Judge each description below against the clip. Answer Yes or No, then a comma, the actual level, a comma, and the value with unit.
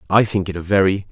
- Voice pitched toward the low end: Yes, very low, 95 Hz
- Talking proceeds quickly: Yes, fast, 270 wpm